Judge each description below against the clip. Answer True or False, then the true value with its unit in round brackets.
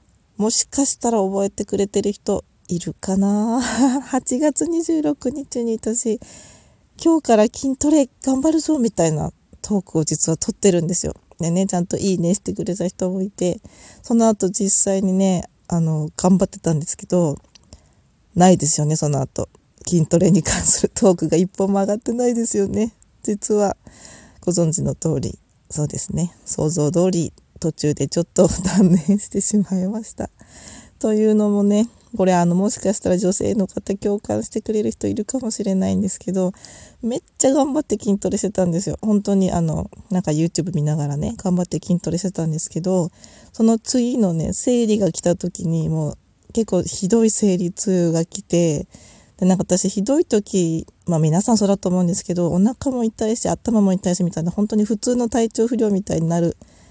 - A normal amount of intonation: True (4.2 semitones)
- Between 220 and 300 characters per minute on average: False (350 characters per minute)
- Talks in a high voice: True (195 Hz)